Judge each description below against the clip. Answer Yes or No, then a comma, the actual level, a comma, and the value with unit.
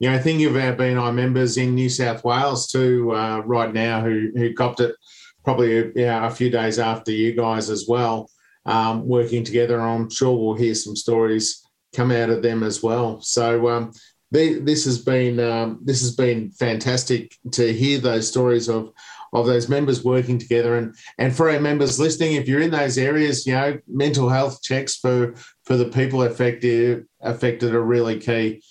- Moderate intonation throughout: No, narrow, 2.1 semitones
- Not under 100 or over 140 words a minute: No, average, 180 wpm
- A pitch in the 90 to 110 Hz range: No, low, 120 Hz